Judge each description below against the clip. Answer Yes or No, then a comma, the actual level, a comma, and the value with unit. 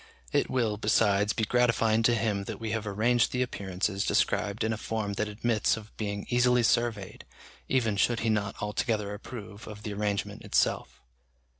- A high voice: No, low, 110 Hz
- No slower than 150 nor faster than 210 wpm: Yes, average, 170 wpm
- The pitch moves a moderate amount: No, narrow, 2.2 semitones